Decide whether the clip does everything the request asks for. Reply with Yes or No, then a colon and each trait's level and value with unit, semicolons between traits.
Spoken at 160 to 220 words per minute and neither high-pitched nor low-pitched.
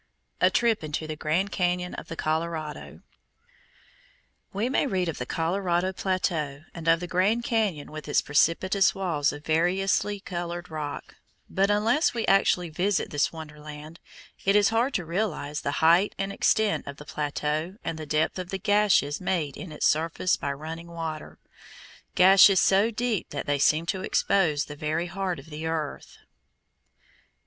Yes: average, 165 wpm; medium, 170 Hz